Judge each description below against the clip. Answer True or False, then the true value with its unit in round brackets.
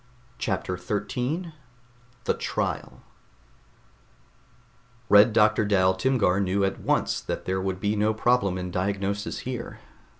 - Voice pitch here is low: True (100 Hz)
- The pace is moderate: False (120 wpm)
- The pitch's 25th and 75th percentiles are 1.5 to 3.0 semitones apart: True (2.6 semitones)